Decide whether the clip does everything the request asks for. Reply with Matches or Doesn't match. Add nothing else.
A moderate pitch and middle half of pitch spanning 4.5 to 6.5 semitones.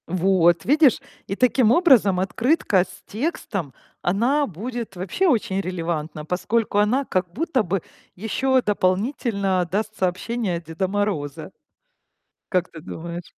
Doesn't match